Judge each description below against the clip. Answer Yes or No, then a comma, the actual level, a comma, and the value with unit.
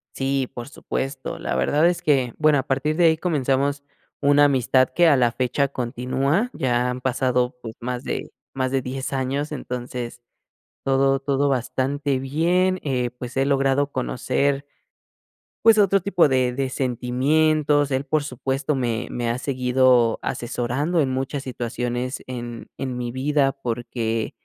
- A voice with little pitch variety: Yes, narrow, 2.3 semitones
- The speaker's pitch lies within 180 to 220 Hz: No, low, 135 Hz